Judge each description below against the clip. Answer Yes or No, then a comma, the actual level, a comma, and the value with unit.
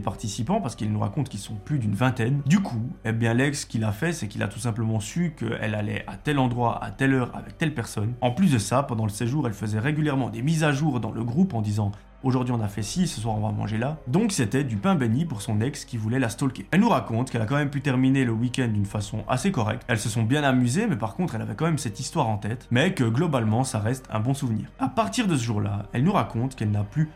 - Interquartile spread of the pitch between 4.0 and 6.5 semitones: Yes, average, 4.4 semitones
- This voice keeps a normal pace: No, fast, 285 wpm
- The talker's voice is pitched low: Yes, low, 120 Hz